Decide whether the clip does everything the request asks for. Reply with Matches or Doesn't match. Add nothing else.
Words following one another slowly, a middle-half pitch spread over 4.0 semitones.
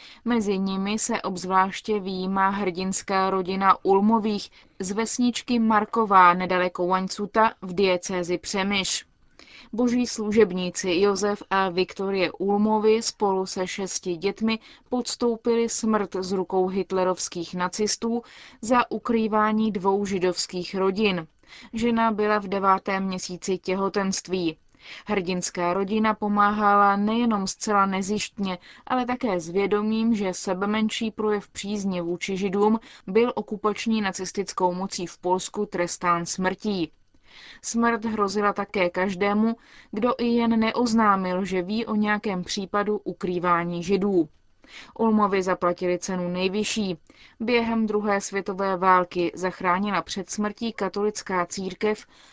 Doesn't match